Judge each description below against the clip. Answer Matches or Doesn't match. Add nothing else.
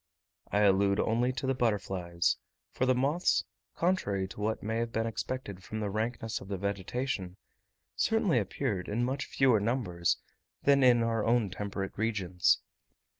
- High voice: Doesn't match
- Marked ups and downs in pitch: Doesn't match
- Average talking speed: Matches